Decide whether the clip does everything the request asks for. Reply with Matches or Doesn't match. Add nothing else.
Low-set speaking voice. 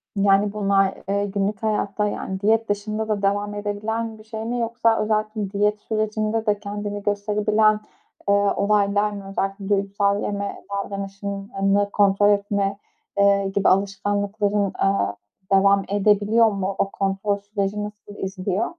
Doesn't match